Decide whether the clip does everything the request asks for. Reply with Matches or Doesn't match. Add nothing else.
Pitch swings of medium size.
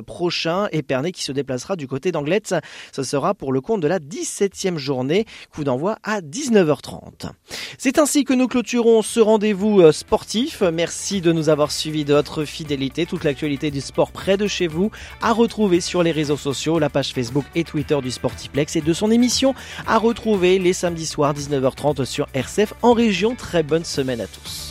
Doesn't match